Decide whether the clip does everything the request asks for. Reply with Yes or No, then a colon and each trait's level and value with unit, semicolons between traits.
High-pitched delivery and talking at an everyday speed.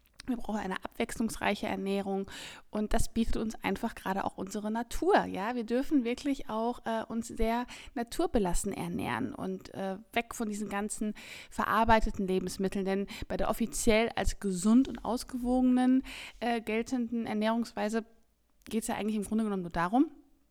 Yes: high, 225 Hz; average, 150 wpm